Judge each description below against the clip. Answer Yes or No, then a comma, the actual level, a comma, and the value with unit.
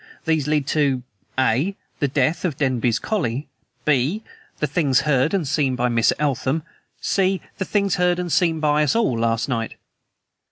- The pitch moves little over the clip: No, average, 5.0 semitones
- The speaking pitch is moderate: Yes, medium, 150 Hz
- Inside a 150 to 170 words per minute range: Yes, average, 165 wpm